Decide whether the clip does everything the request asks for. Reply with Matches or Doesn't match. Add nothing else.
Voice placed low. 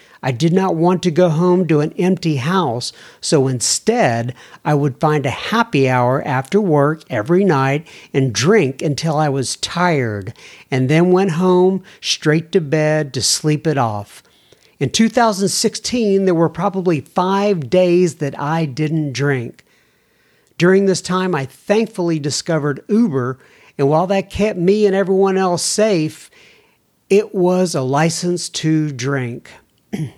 Doesn't match